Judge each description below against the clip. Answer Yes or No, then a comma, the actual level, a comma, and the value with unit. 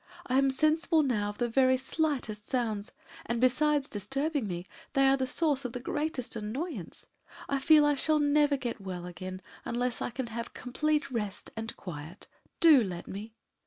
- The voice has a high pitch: Yes, very high, 255 Hz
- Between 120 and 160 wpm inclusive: No, average, 175 wpm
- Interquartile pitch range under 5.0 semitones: No, average, 5.3 semitones